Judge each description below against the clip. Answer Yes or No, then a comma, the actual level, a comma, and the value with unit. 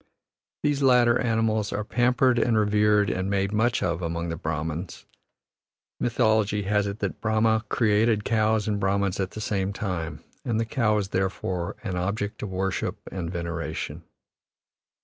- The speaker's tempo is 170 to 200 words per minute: No, average, 150 wpm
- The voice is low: Yes, low, 105 Hz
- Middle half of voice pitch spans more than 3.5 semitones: No, average, 2.9 semitones